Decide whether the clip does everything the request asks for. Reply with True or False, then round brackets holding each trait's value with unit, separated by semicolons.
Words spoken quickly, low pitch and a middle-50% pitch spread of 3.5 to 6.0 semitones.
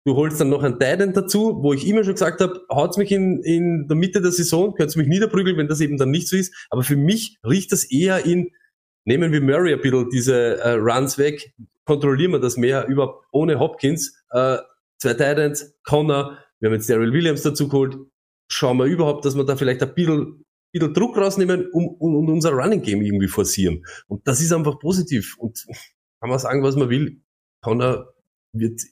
False (205 wpm; 150 Hz; 4.6 semitones)